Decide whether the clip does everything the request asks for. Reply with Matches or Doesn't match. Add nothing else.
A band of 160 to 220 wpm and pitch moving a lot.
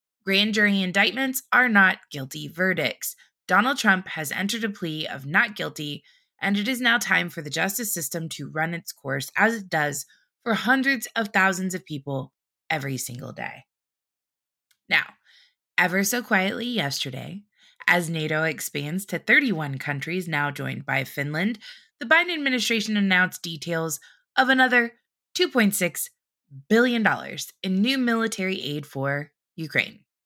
Doesn't match